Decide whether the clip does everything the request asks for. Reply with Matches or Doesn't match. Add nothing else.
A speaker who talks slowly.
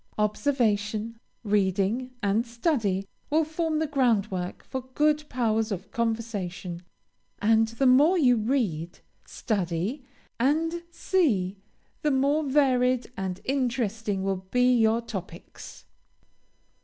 Matches